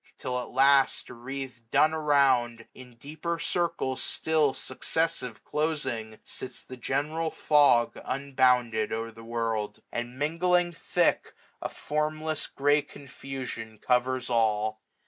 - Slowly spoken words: Yes, slow, 120 wpm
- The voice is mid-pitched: No, low, 130 Hz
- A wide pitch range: No, average, 4.3 semitones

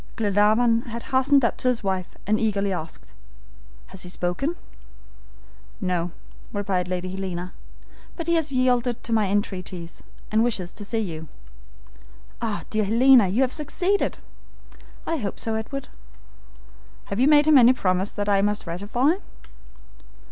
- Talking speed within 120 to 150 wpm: Yes, average, 145 wpm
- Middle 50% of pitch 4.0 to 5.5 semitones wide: Yes, average, 5.1 semitones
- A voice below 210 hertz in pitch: No, high, 215 Hz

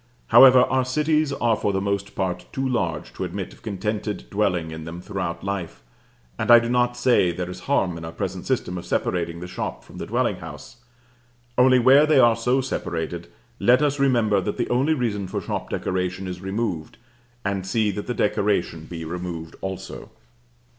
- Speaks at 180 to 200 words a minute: Yes, average, 190 wpm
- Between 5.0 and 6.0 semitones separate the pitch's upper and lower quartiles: Yes, wide, 5.5 semitones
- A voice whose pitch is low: Yes, low, 100 Hz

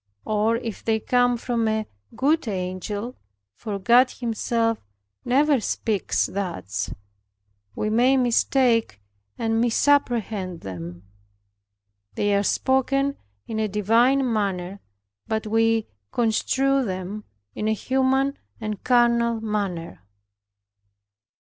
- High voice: Yes, high, 225 Hz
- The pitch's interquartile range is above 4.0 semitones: No, average, 3.3 semitones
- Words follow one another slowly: Yes, slow, 105 wpm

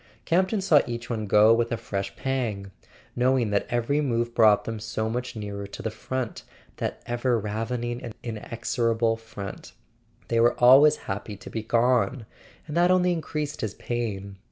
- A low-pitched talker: Yes, low, 115 Hz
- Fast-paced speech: No, average, 165 wpm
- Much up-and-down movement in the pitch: No, average, 2.9 semitones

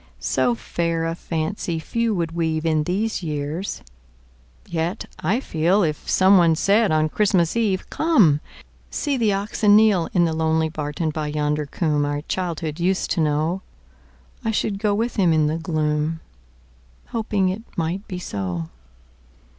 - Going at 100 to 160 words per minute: Yes, average, 140 wpm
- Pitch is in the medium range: Yes, medium, 165 Hz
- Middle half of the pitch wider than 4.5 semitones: No, average, 4.2 semitones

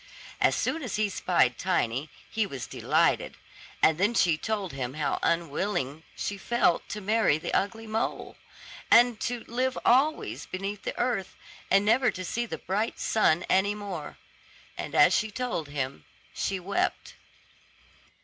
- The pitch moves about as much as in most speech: No, wide, 5.7 semitones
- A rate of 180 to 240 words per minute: No, average, 150 wpm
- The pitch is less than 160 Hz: No, high, 200 Hz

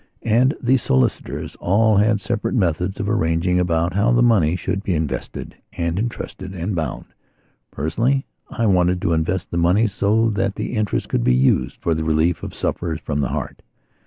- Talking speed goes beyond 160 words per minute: Yes, average, 180 wpm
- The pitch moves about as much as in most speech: Yes, average, 4.7 semitones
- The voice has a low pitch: Yes, very low, 95 Hz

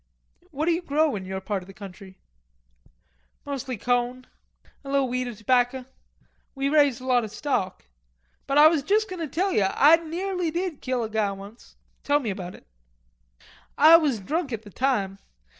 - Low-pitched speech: No, very high, 260 Hz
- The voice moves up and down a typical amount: No, wide, 6.4 semitones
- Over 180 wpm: Yes, average, 190 wpm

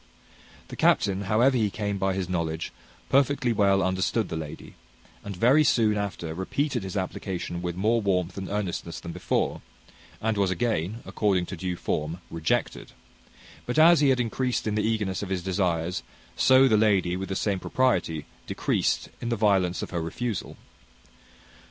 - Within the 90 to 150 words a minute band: No, average, 165 wpm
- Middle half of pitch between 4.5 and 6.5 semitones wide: No, average, 3.9 semitones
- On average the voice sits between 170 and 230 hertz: No, low, 100 Hz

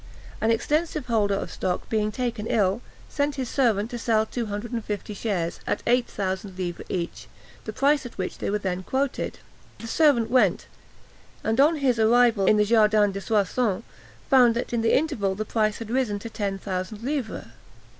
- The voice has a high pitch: Yes, high, 220 Hz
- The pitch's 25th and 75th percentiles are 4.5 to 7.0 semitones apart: No, average, 3.3 semitones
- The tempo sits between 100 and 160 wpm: No, average, 185 wpm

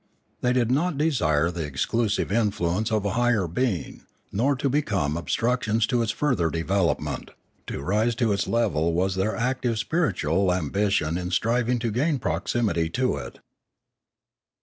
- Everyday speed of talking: Yes, average, 150 wpm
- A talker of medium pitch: No, low, 105 Hz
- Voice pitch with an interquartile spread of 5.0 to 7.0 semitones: Yes, wide, 5.5 semitones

